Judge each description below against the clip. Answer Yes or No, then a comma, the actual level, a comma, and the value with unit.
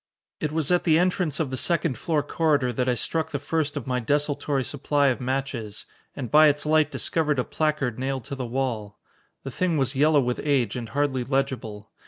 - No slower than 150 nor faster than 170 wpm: No, fast, 205 wpm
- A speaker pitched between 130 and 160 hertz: Yes, medium, 140 Hz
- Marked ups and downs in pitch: No, average, 3.2 semitones